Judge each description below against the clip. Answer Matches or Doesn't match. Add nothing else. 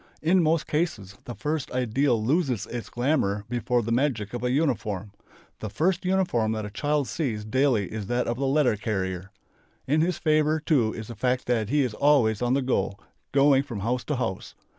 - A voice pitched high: Doesn't match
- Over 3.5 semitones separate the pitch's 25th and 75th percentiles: Matches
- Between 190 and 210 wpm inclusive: Matches